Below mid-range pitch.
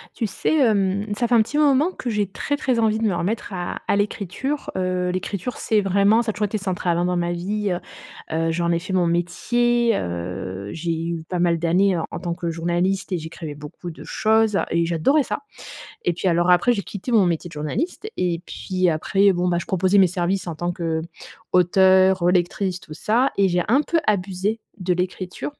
No: medium, 185 Hz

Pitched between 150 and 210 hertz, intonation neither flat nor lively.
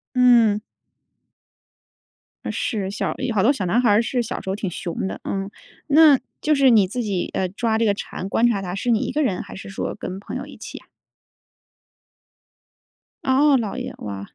No: high, 220 Hz; average, 4.4 semitones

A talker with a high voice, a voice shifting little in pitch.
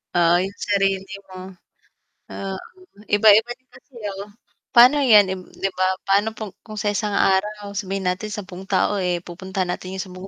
Yes: high, 195 Hz; narrow, 1.9 semitones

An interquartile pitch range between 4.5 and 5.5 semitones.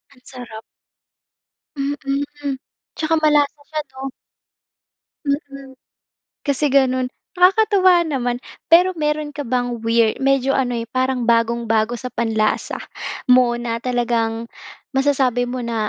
No: average, 3.3 semitones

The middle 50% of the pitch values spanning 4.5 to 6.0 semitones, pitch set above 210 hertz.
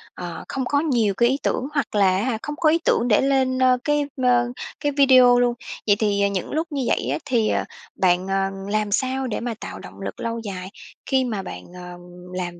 Yes: average, 4.9 semitones; high, 240 Hz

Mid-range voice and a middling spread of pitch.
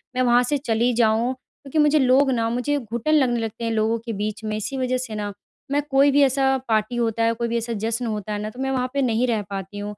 No: high, 235 Hz; average, 3.0 semitones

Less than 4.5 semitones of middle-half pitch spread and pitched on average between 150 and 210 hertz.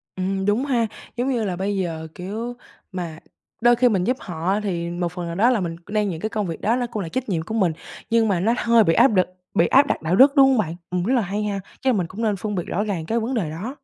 No: average, 4.8 semitones; high, 205 Hz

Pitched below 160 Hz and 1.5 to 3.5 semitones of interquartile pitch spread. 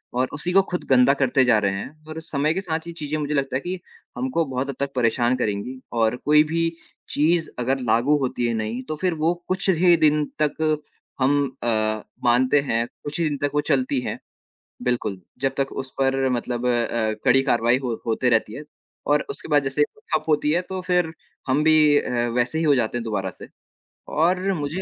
No: medium, 140 Hz; average, 4.0 semitones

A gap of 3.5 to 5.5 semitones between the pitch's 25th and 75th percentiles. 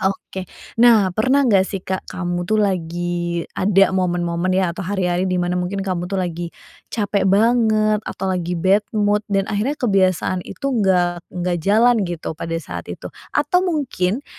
No: average, 2.9 semitones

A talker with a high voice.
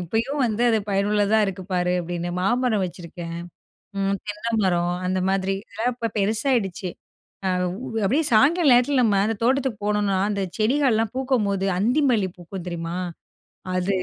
Yes: high, 205 Hz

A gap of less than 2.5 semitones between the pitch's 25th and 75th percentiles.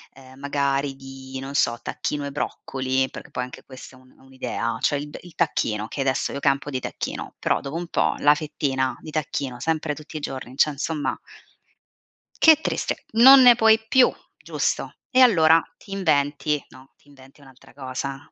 No: average, 2.8 semitones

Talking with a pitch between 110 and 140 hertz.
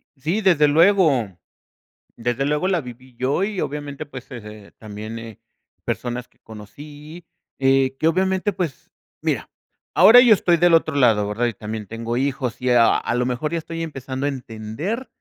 Yes: low, 135 Hz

